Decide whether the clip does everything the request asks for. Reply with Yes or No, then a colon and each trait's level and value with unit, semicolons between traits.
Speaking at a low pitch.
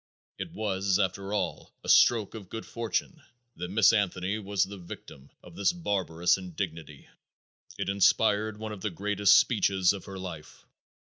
Yes: low, 100 Hz